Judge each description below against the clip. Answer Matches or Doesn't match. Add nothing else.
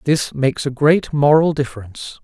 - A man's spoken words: Matches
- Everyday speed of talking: Matches